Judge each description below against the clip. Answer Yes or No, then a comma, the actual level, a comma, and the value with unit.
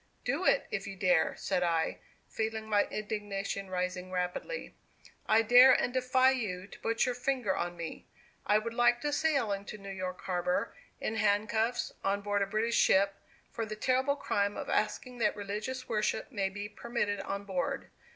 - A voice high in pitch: Yes, high, 210 Hz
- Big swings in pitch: No, average, 3.5 semitones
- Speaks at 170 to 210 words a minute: Yes, average, 175 wpm